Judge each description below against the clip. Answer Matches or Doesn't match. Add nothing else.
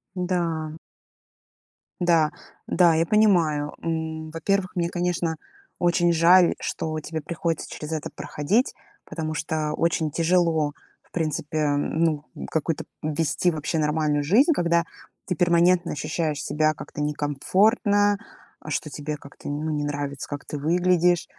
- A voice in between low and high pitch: Matches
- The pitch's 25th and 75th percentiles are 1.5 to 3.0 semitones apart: Matches